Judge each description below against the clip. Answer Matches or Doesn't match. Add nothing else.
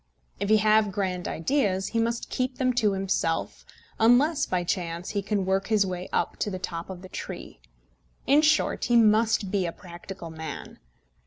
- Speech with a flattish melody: Doesn't match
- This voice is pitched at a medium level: Doesn't match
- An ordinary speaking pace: Matches